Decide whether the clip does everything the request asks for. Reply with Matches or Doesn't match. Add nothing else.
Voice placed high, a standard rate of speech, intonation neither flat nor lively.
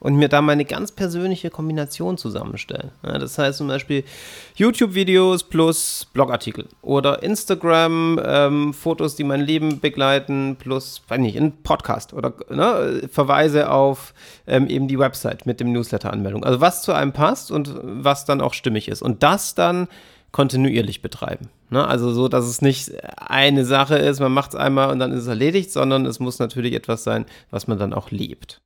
Doesn't match